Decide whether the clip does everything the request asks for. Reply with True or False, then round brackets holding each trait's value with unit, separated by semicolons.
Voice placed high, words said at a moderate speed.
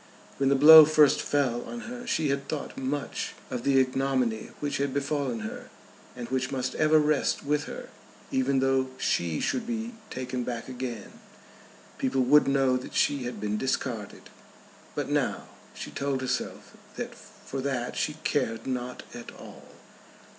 False (135 Hz; 160 wpm)